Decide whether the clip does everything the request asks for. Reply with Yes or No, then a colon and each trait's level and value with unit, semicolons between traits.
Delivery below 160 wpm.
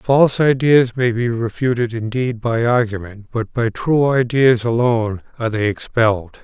Yes: average, 150 wpm